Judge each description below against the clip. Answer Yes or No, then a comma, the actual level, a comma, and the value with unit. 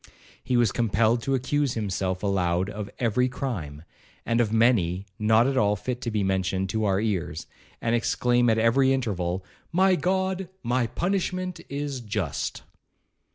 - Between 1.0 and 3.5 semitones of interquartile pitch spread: No, average, 5.0 semitones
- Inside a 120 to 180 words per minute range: Yes, average, 155 wpm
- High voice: No, low, 115 Hz